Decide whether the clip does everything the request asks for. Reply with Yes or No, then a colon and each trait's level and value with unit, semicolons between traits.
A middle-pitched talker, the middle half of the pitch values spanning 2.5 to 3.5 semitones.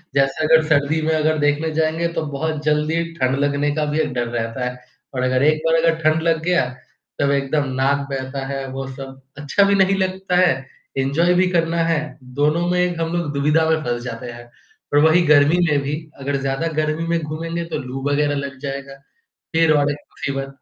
Yes: medium, 150 Hz; average, 3.1 semitones